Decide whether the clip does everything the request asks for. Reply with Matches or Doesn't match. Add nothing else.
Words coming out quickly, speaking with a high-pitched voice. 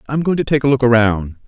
Doesn't match